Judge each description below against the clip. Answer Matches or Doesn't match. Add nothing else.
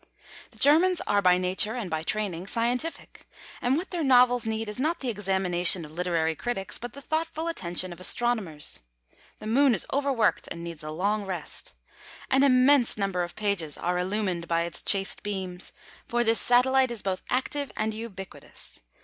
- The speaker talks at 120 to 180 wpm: Matches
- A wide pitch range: Matches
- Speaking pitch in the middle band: Doesn't match